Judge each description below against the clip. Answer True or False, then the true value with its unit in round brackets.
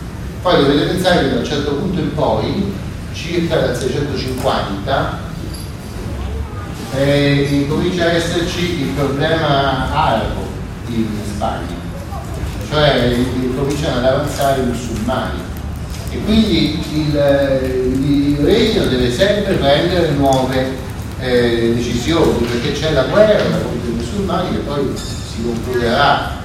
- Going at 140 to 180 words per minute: False (115 wpm)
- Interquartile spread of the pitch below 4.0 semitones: False (5.1 semitones)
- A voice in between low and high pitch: False (130 Hz)